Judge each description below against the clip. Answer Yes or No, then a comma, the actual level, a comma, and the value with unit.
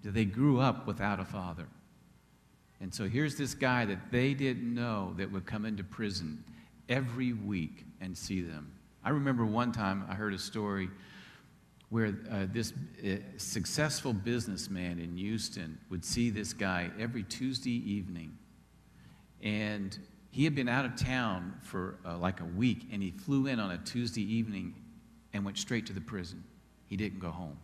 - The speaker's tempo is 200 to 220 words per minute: No, average, 170 wpm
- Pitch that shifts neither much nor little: Yes, average, 4.2 semitones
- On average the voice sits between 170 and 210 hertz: No, low, 105 Hz